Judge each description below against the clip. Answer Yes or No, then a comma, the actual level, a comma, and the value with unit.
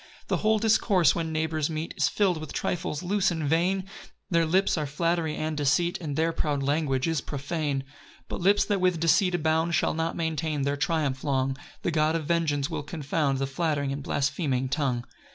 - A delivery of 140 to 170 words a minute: No, average, 195 wpm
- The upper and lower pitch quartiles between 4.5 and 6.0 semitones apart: No, average, 3.0 semitones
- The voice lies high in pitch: No, medium, 160 Hz